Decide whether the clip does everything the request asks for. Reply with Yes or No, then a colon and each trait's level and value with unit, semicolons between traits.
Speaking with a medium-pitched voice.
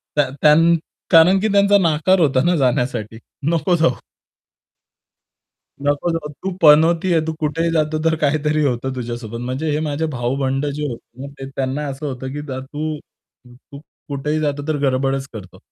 Yes: medium, 145 Hz